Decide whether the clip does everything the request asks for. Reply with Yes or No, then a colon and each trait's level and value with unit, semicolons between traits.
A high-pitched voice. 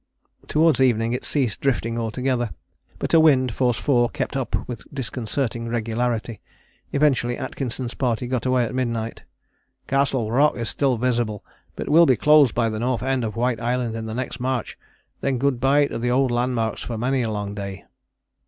No: low, 125 Hz